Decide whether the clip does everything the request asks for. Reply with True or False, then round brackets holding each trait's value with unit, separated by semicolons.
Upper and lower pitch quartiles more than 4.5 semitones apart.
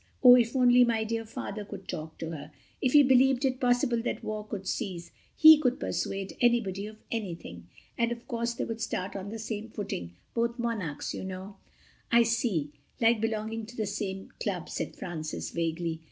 False (3.9 semitones)